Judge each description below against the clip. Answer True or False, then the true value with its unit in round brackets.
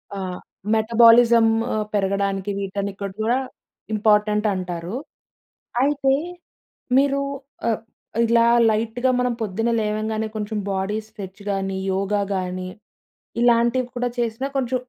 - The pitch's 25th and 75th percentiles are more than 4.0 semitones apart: False (3.0 semitones)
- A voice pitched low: False (215 Hz)